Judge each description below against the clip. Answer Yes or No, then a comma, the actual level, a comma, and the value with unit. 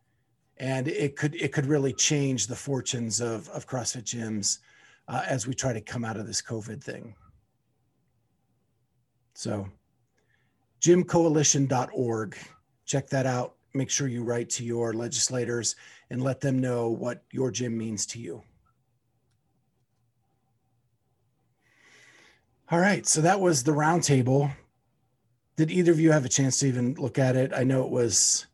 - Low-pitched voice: Yes, low, 125 Hz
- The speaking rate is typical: Yes, average, 145 wpm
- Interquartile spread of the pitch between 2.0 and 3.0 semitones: Yes, narrow, 2.6 semitones